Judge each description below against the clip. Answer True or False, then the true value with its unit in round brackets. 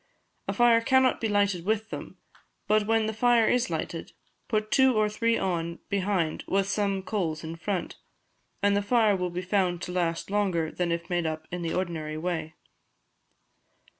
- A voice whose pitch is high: True (195 Hz)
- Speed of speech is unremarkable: True (175 wpm)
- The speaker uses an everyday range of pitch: True (4.0 semitones)